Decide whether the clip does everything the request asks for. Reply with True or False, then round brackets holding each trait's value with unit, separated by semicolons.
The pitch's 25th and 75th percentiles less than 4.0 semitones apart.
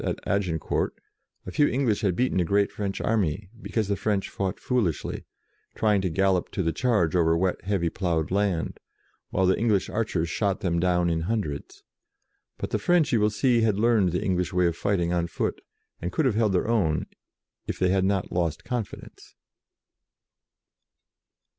True (3.5 semitones)